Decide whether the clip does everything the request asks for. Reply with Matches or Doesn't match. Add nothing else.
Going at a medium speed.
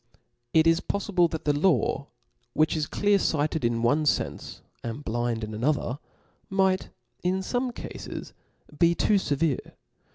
Matches